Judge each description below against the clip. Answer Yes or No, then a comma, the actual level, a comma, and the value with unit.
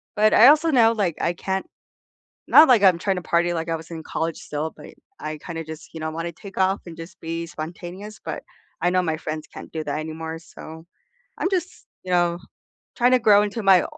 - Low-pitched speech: No, medium, 175 Hz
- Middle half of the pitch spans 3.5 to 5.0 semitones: Yes, average, 4.0 semitones